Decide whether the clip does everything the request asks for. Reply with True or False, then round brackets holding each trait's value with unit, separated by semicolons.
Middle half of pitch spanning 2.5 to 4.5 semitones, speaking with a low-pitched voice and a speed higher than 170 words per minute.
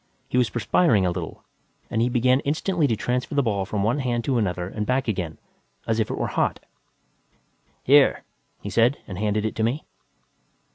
True (3.7 semitones; 115 Hz; 190 wpm)